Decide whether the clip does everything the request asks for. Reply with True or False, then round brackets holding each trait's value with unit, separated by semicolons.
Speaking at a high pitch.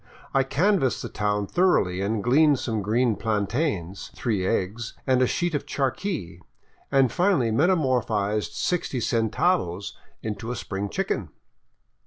False (120 Hz)